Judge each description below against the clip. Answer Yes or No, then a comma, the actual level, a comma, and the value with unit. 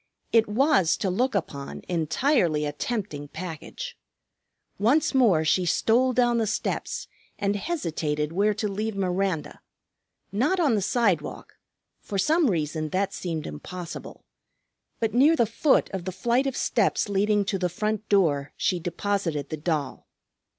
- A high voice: Yes, high, 195 Hz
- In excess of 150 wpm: No, average, 145 wpm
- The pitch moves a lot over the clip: Yes, wide, 6.0 semitones